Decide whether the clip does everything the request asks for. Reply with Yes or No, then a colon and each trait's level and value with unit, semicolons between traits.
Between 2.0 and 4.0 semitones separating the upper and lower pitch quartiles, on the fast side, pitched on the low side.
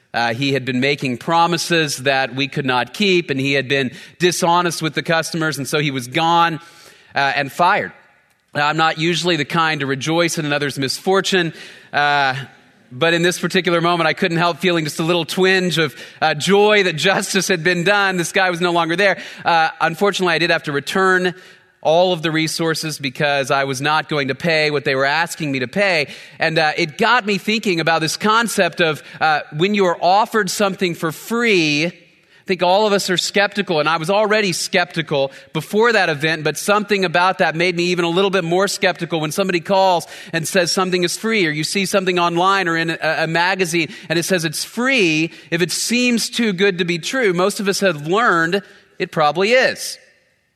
No: average, 3.3 semitones; fast, 210 wpm; medium, 170 Hz